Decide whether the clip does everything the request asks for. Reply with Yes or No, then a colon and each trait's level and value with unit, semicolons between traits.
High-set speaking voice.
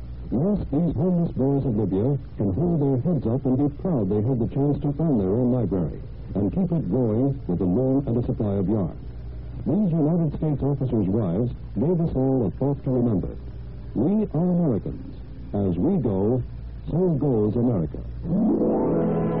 No: low, 130 Hz